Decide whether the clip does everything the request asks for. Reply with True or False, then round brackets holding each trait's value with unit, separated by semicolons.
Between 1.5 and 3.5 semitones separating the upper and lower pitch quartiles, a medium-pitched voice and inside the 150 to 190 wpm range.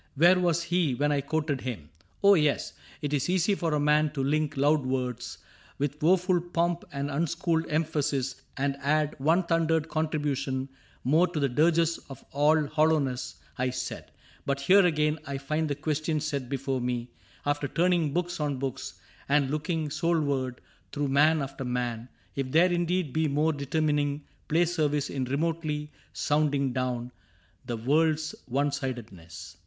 True (2.8 semitones; 150 Hz; 160 wpm)